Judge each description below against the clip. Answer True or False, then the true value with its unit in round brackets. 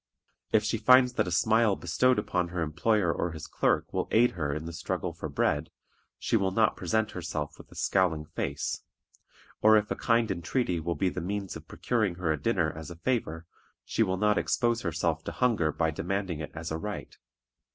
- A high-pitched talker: False (90 Hz)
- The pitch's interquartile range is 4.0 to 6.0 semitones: True (4.8 semitones)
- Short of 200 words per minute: False (205 wpm)